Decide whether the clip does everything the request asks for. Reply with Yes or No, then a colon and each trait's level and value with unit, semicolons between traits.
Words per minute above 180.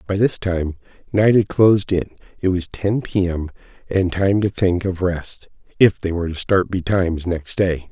Yes: average, 195 wpm